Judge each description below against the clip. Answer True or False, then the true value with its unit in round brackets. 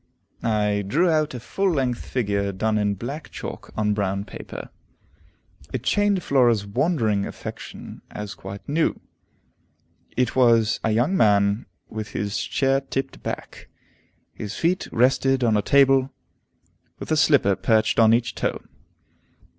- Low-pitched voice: True (115 Hz)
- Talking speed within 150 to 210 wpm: False (140 wpm)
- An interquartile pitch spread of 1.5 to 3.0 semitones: False (4.6 semitones)